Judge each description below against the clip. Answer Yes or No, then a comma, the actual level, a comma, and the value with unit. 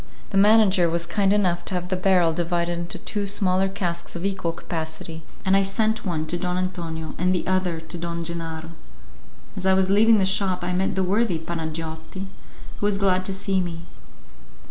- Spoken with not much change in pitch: Yes, narrow, 2.3 semitones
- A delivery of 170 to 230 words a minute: Yes, average, 190 wpm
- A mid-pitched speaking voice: Yes, medium, 180 Hz